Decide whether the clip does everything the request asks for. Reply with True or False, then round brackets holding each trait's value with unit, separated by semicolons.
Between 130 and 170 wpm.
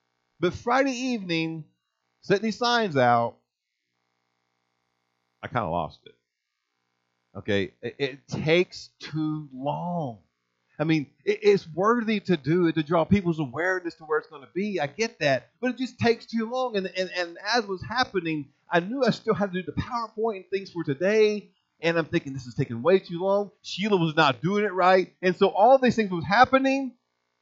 False (185 wpm)